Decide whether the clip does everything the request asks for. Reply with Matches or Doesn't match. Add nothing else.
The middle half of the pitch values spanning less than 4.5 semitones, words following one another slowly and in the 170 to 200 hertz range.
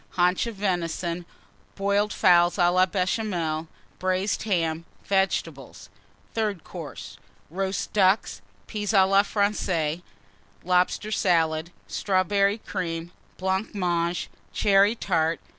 Matches